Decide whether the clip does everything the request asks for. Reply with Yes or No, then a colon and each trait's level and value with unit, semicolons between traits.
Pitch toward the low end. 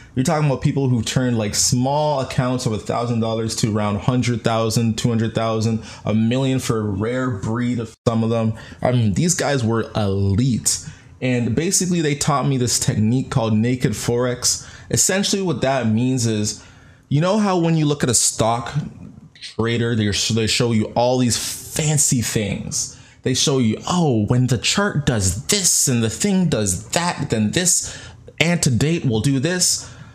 Yes: low, 125 Hz